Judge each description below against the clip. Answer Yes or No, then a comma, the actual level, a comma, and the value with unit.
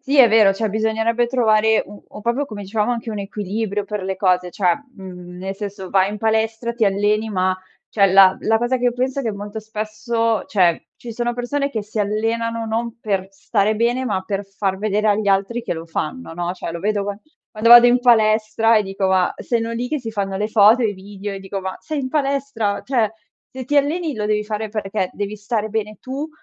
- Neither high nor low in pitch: No, high, 215 Hz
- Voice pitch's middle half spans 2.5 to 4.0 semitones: Yes, average, 2.8 semitones